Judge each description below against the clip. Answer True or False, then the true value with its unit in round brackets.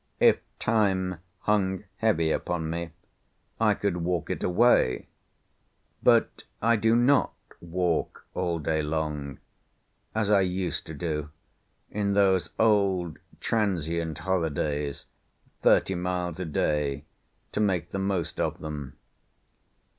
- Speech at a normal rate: False (115 wpm)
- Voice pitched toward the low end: True (90 Hz)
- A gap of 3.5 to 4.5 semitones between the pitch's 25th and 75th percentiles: True (3.8 semitones)